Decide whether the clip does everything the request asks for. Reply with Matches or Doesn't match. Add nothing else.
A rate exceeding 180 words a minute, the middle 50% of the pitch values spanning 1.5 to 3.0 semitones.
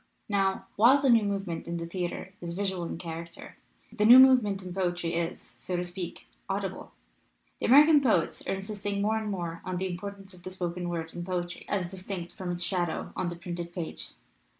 Matches